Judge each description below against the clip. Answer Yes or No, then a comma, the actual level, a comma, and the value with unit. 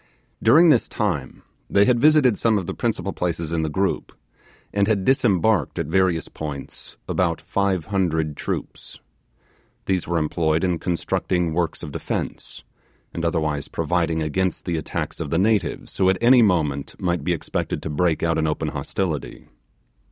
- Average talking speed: Yes, average, 160 wpm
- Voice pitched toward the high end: No, very low, 90 Hz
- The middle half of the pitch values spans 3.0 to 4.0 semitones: Yes, average, 3.6 semitones